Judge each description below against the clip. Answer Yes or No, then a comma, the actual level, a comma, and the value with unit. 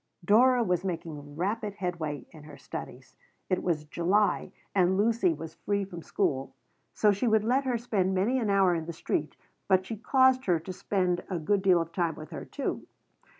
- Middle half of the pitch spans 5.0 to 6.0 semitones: No, average, 4.1 semitones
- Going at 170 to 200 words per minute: Yes, average, 195 wpm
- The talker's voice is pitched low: No, medium, 185 Hz